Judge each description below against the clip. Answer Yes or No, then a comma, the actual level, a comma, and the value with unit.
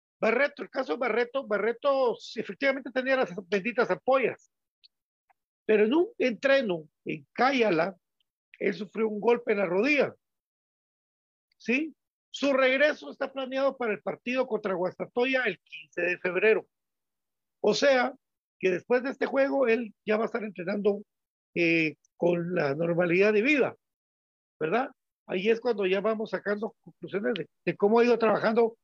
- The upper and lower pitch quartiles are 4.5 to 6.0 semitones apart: Yes, average, 5.2 semitones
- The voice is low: No, high, 220 Hz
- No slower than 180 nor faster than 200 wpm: No, average, 150 wpm